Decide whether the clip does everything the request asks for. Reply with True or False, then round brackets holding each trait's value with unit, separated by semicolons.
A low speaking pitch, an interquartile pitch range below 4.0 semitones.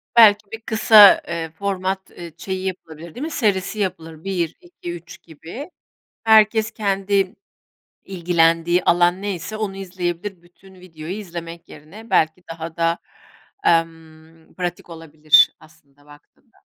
False (175 Hz; 3.4 semitones)